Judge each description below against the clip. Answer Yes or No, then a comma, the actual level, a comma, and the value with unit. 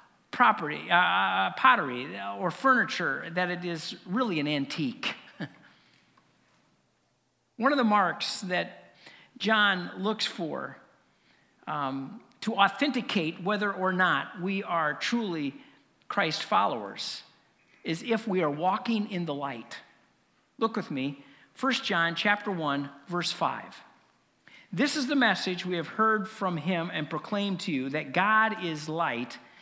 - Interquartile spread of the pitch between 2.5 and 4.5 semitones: No, average, 5.0 semitones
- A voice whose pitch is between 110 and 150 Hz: No, medium, 185 Hz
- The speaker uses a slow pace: Yes, slow, 130 wpm